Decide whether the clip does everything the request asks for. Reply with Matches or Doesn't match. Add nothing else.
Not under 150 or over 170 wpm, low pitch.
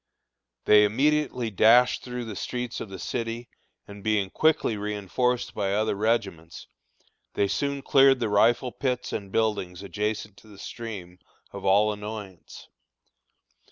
Doesn't match